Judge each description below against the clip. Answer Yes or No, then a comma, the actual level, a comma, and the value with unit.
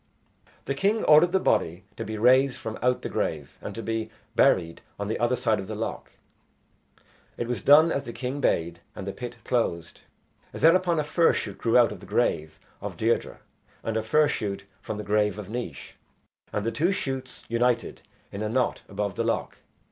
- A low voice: Yes, low, 115 Hz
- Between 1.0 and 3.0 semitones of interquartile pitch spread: No, average, 4.5 semitones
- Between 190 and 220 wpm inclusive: Yes, average, 195 wpm